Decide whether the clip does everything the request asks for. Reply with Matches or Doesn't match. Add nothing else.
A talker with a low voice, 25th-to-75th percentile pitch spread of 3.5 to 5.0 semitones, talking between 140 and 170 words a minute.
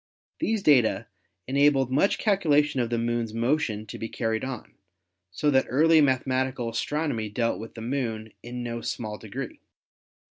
Matches